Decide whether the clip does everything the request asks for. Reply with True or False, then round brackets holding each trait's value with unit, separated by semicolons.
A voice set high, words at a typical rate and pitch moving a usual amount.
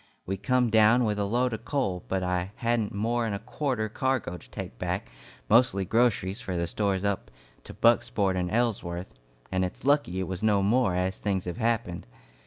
False (100 Hz; 190 wpm; 4.1 semitones)